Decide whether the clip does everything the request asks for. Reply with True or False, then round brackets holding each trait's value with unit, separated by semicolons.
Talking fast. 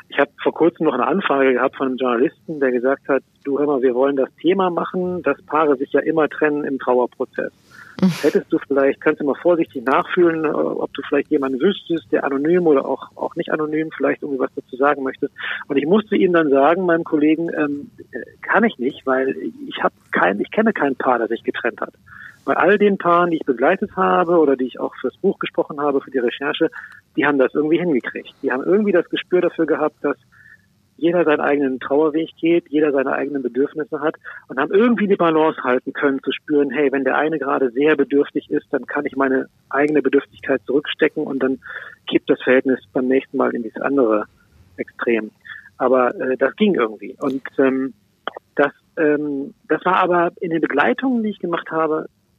True (205 wpm)